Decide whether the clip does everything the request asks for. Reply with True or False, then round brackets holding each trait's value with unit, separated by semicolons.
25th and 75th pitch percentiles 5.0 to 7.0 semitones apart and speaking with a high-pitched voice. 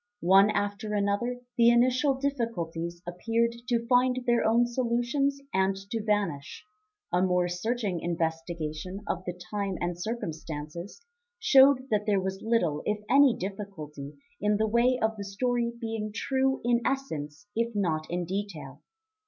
True (5.3 semitones; 210 Hz)